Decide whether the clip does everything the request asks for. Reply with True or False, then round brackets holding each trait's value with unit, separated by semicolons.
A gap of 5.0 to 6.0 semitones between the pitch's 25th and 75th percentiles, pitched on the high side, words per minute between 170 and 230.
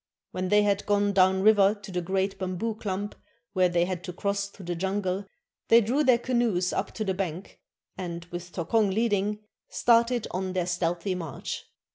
False (2.4 semitones; 195 Hz; 180 wpm)